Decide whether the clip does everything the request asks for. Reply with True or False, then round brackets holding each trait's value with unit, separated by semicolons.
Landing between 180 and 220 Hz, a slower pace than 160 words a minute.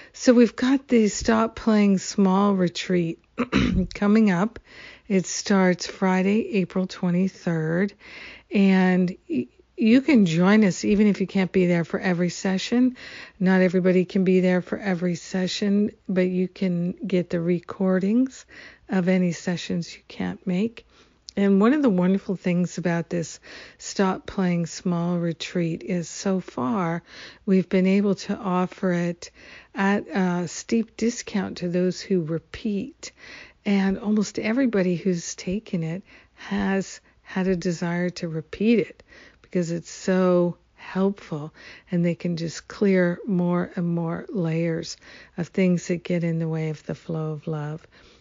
True (185 Hz; 145 wpm)